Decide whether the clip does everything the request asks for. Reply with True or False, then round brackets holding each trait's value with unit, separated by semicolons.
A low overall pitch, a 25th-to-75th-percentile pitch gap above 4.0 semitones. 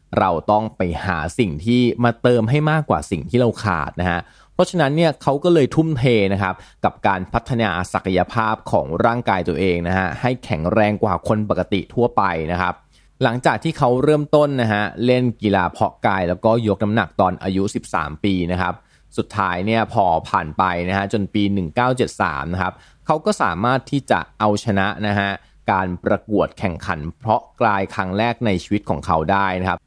True (105 Hz; 4.6 semitones)